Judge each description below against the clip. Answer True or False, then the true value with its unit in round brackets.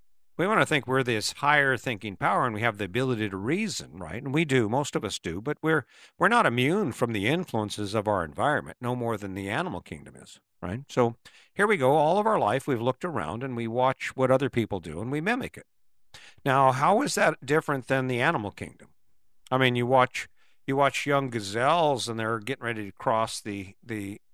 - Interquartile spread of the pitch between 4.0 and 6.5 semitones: True (4.5 semitones)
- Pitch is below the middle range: True (125 Hz)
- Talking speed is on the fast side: True (220 wpm)